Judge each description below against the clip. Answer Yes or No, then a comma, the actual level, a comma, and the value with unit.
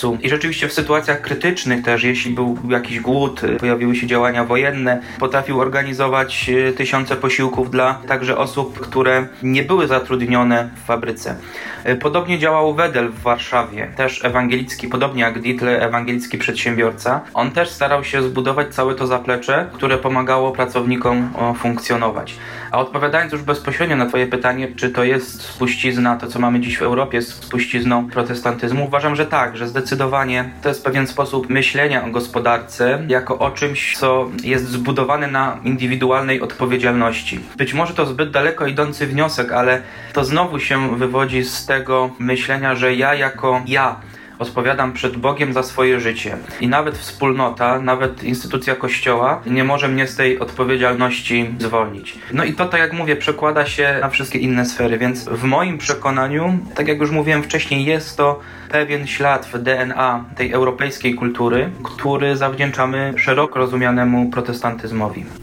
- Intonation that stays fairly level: Yes, narrow, 2.1 semitones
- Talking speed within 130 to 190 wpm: Yes, average, 150 wpm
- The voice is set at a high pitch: No, low, 130 Hz